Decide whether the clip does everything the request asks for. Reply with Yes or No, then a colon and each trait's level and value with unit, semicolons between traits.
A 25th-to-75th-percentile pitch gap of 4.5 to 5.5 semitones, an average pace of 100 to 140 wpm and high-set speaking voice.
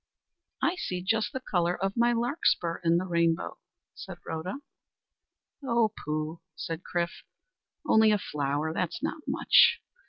No: average, 5.0 semitones; slow, 135 wpm; medium, 180 Hz